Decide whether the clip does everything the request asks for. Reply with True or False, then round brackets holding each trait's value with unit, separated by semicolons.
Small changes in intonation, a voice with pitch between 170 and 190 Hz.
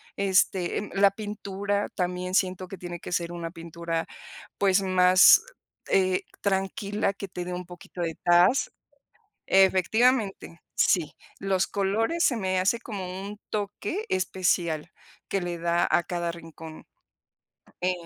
True (2.3 semitones; 185 Hz)